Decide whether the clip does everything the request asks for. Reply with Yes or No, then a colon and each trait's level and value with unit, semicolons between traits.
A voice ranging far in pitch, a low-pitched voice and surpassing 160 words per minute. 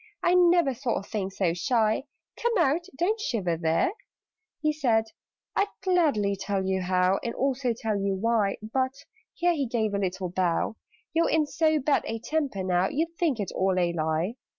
No: wide, 8.1 semitones; high, 225 Hz; average, 180 wpm